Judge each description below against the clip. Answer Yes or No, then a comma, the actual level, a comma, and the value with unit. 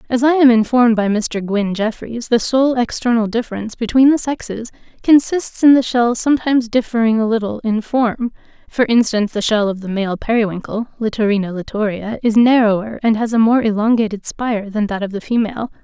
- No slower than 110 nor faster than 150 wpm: No, average, 180 wpm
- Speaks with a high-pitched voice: Yes, high, 225 Hz